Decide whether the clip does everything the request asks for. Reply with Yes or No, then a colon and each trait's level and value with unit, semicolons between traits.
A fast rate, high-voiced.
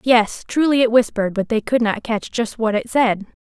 Yes: fast, 225 wpm; high, 230 Hz